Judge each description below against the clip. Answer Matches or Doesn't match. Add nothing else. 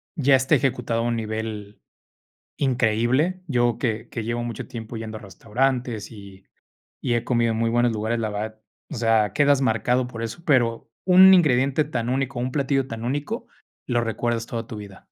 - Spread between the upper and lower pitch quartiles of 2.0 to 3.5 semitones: Matches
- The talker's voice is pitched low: Matches